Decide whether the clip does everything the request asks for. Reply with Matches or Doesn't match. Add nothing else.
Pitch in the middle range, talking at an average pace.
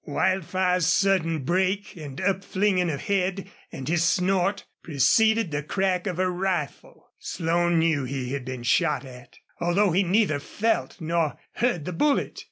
Matches